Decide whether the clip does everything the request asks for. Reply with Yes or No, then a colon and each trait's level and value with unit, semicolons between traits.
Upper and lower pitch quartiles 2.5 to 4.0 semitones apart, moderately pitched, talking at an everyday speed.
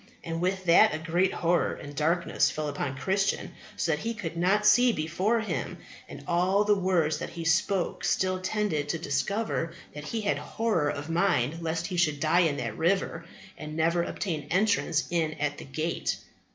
Yes: average, 3.6 semitones; medium, 170 Hz; average, 185 wpm